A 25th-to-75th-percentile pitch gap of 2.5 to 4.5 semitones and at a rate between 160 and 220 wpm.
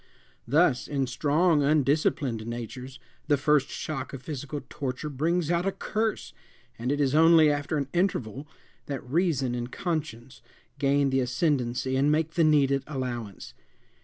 No: average, 3.3 semitones; average, 145 wpm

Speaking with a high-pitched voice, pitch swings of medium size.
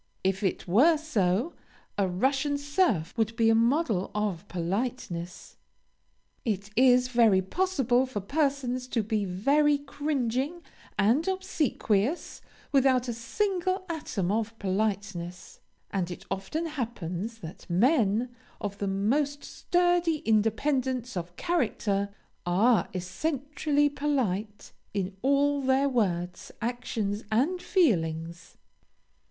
No: high, 235 Hz; wide, 6.5 semitones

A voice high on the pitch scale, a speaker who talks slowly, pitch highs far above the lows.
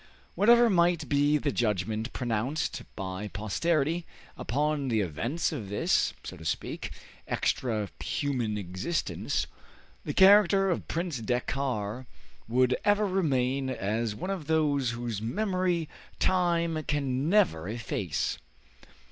No: low, 135 Hz; slow, 115 wpm; wide, 7.3 semitones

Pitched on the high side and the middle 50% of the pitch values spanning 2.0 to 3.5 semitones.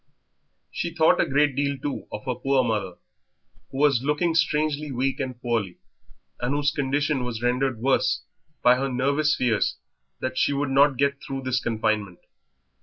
No: low, 135 Hz; average, 2.7 semitones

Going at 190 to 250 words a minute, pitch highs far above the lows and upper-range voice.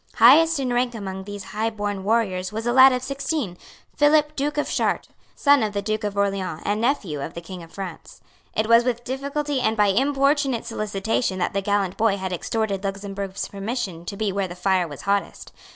No: average, 200 wpm; average, 4.6 semitones; high, 210 Hz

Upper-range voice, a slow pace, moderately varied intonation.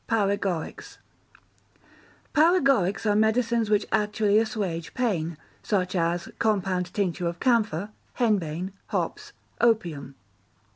Yes: high, 200 Hz; slow, 95 wpm; average, 4.1 semitones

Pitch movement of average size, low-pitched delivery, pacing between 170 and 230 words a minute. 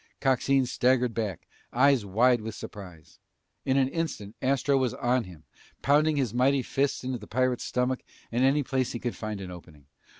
Yes: average, 3.6 semitones; low, 125 Hz; average, 175 wpm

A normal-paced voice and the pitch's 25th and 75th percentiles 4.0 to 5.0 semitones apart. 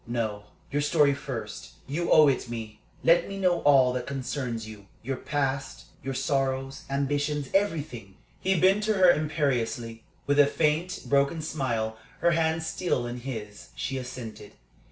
Yes: average, 155 wpm; average, 4.4 semitones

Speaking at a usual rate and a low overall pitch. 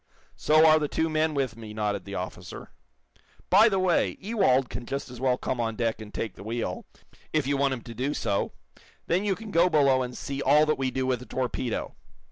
No: fast, 225 wpm; low, 130 Hz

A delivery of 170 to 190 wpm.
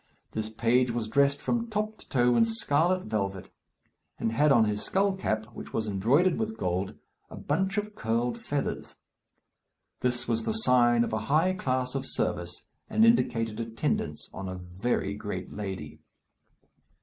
No: average, 160 wpm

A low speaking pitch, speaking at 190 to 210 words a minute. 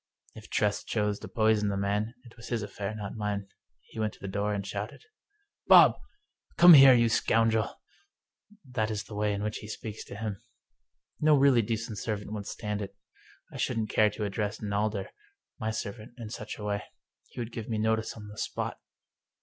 Yes: low, 110 Hz; average, 200 wpm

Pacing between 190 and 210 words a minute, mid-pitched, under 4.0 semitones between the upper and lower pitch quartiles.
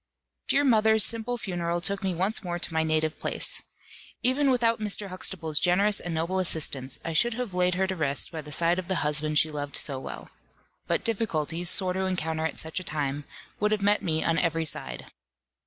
No: fast, 205 wpm; medium, 175 Hz; average, 4.3 semitones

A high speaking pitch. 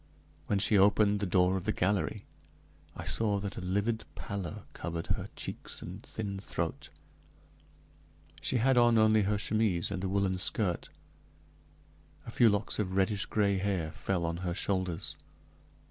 No: low, 100 Hz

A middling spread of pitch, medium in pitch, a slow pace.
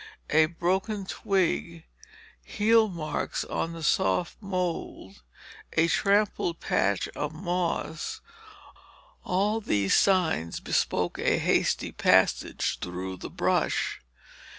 Yes: average, 4.1 semitones; medium, 170 Hz; slow, 100 wpm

